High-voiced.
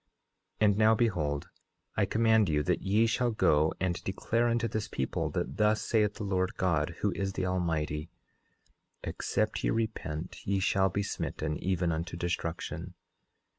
No: very low, 95 Hz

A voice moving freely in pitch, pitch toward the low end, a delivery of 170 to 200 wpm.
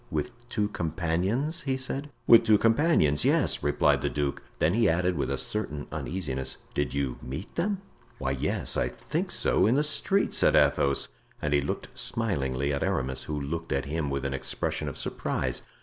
Yes: wide, 8.5 semitones; very low, 80 Hz; average, 180 wpm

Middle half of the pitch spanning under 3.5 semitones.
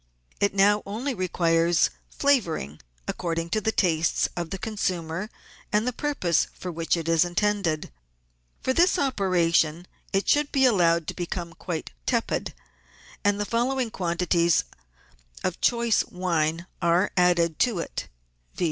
No: average, 4.1 semitones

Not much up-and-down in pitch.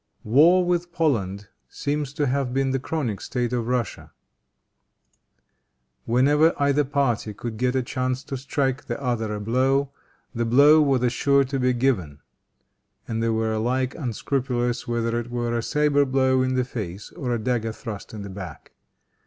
No: average, 3.2 semitones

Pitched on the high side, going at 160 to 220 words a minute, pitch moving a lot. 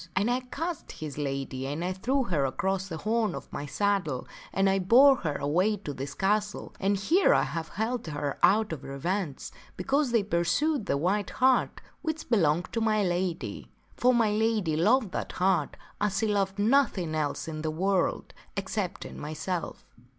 Yes: high, 195 Hz; average, 180 wpm; wide, 5.7 semitones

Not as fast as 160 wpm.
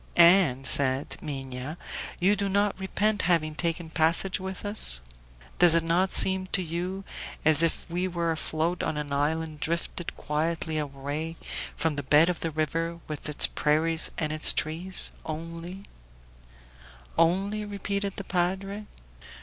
Yes: average, 145 wpm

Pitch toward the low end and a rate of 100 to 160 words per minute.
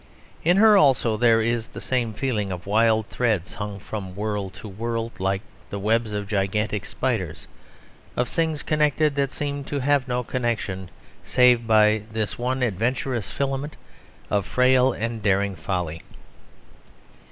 Yes: low, 115 Hz; average, 145 wpm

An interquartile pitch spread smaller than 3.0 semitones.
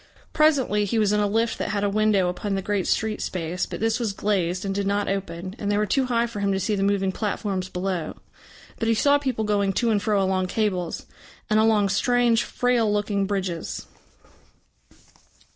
Yes: narrow, 2.4 semitones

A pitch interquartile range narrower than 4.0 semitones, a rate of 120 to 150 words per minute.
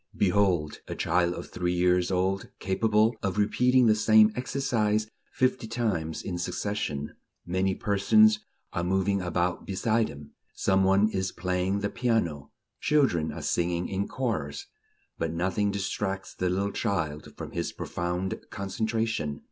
Yes: average, 3.5 semitones; average, 140 wpm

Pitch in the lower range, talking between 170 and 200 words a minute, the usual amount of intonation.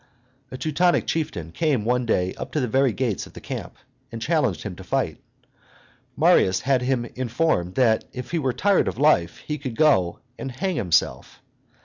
No: low, 125 Hz; average, 180 wpm; wide, 6.2 semitones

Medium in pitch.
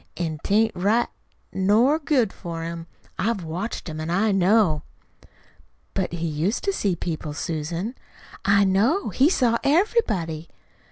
No: high, 195 Hz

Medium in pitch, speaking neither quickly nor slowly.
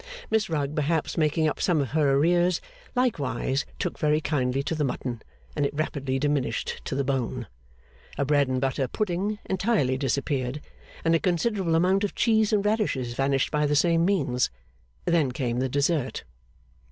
Yes: medium, 150 Hz; average, 165 wpm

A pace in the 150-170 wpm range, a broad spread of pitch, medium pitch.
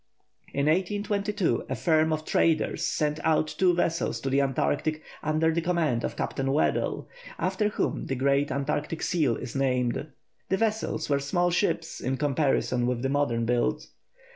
No: average, 160 wpm; average, 3.9 semitones; medium, 155 Hz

